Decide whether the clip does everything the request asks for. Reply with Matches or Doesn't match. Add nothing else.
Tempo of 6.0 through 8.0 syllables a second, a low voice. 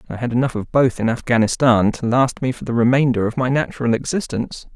Matches